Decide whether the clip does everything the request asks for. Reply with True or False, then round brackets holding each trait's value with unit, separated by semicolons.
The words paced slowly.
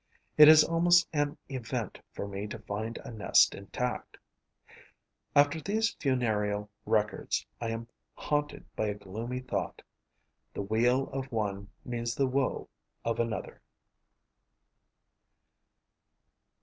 True (115 wpm)